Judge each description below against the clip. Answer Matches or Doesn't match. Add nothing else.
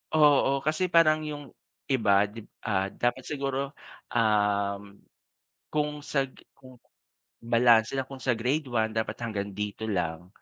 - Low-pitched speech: Matches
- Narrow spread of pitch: Doesn't match